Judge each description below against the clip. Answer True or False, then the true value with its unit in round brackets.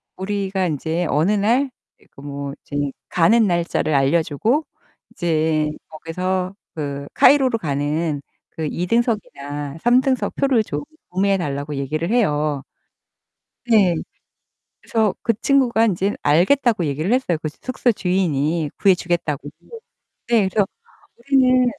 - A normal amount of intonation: False (6.9 semitones)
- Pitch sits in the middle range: True (180 Hz)